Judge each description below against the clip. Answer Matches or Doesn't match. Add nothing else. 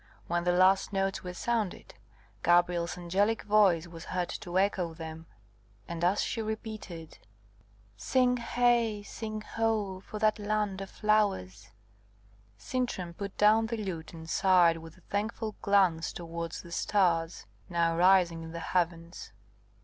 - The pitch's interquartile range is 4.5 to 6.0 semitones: Doesn't match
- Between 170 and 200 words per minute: Doesn't match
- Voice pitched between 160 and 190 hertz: Matches